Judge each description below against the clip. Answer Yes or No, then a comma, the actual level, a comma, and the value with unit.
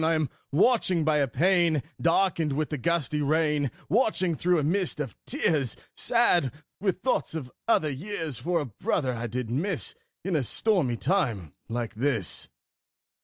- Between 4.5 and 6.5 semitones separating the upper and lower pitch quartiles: Yes, average, 5.2 semitones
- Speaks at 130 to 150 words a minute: No, average, 160 wpm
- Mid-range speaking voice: Yes, medium, 155 Hz